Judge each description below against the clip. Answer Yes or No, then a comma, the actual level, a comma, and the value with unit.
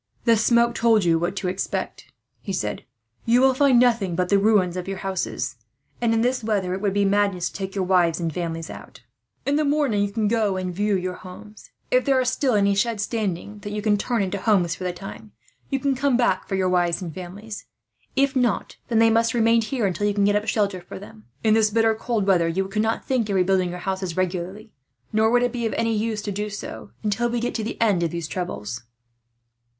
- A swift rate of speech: Yes, fast, 230 wpm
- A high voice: Yes, high, 205 Hz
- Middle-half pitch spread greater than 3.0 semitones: Yes, average, 3.7 semitones